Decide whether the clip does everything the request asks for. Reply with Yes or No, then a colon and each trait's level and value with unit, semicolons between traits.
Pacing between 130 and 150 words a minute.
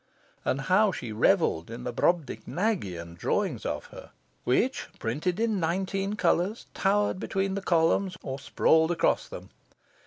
Yes: slow, 135 wpm